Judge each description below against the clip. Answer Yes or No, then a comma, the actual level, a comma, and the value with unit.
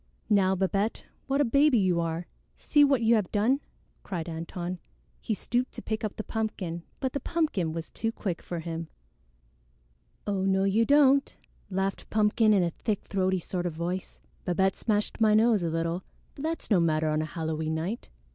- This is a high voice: Yes, high, 195 Hz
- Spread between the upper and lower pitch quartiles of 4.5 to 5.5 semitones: Yes, average, 4.8 semitones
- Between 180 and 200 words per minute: Yes, average, 185 wpm